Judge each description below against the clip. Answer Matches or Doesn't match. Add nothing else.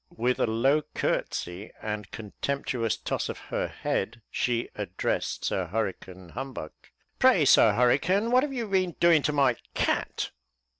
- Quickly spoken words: Doesn't match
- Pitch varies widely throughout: Matches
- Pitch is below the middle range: Matches